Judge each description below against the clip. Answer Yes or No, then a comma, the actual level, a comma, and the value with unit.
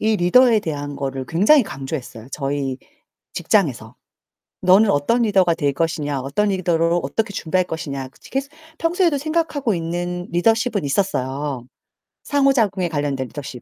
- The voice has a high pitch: No, medium, 175 Hz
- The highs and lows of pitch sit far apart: Yes, wide, 7.4 semitones